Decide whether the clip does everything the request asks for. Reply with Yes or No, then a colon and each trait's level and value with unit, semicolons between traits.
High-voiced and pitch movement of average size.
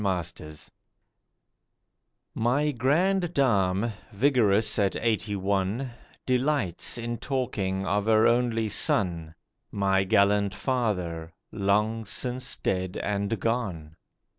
No: low, 105 Hz; average, 4.1 semitones